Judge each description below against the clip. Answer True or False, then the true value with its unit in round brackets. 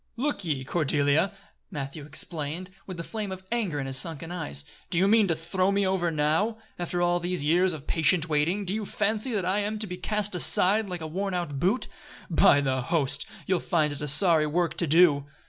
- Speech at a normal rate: False (215 wpm)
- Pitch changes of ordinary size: True (4.3 semitones)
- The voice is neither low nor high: True (175 Hz)